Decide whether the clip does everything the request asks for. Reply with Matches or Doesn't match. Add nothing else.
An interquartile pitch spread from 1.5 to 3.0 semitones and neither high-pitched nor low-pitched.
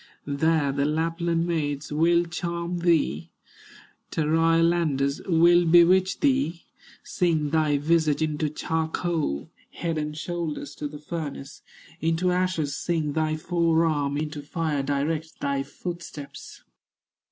Matches